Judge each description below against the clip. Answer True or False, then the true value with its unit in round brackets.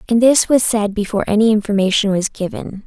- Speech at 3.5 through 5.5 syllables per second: False (6.0 syllables/s)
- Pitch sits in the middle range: False (210 Hz)